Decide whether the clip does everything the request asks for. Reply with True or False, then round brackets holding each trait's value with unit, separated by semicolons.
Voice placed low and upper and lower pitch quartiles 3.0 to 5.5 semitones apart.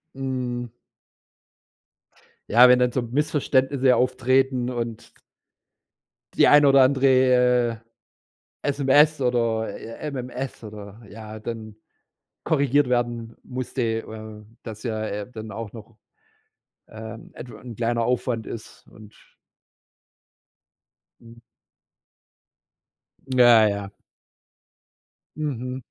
False (120 Hz; 2.6 semitones)